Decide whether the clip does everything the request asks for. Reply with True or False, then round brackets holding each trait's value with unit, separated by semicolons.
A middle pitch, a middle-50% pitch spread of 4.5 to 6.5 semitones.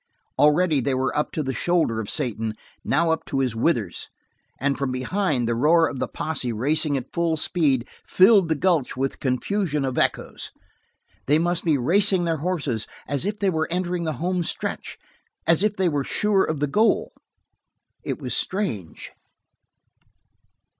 True (155 Hz; 5.0 semitones)